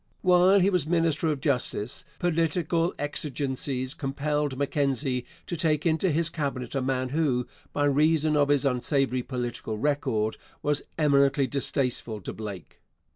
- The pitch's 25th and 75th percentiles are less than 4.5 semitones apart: Yes, average, 3.4 semitones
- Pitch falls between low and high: Yes, medium, 145 Hz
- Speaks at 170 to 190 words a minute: No, slow, 135 wpm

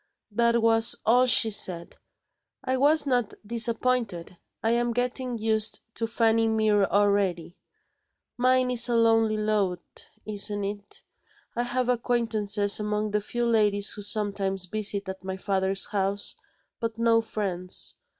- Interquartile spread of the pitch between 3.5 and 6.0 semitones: No, narrow, 2.6 semitones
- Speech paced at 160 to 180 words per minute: No, slow, 135 wpm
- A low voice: No, high, 215 Hz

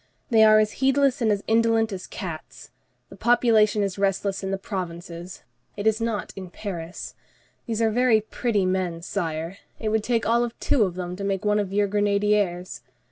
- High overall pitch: Yes, high, 205 Hz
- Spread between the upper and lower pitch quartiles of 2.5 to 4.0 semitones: Yes, average, 3.2 semitones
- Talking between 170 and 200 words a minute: Yes, average, 190 wpm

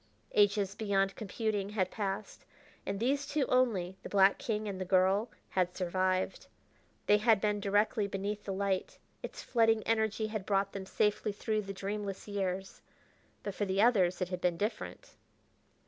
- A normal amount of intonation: No, narrow, 1.9 semitones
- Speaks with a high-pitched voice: Yes, high, 200 Hz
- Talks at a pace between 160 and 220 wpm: Yes, average, 165 wpm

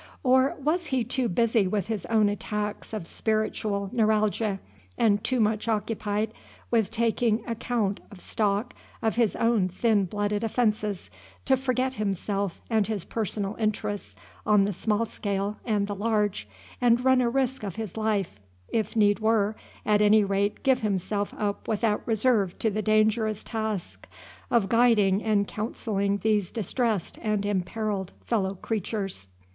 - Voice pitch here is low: No, high, 215 Hz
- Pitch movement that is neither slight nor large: No, narrow, 2.1 semitones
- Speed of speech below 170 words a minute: Yes, average, 150 wpm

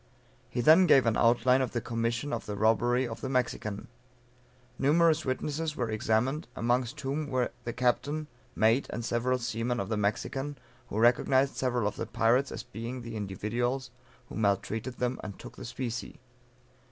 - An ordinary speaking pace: Yes, average, 165 wpm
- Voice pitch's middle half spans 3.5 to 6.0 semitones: No, average, 2.7 semitones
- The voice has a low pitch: Yes, low, 120 Hz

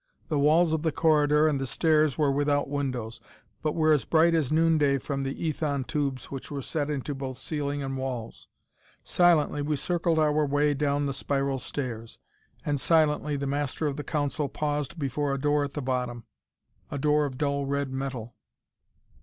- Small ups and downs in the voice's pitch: Yes, narrow, 1.9 semitones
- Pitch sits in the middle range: Yes, medium, 145 Hz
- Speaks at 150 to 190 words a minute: Yes, average, 180 wpm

